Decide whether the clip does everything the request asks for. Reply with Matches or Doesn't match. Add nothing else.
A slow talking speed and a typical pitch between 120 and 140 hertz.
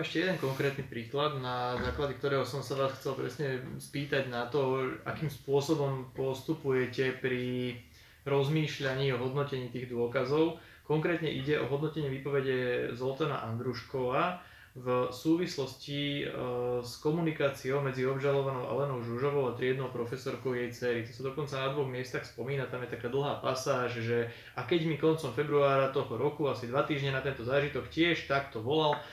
Doesn't match